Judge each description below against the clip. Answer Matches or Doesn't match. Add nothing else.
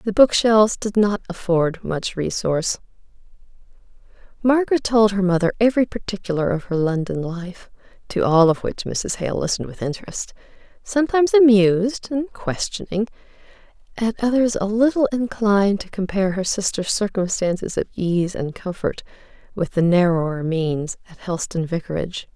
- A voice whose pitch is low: Doesn't match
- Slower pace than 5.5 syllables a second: Matches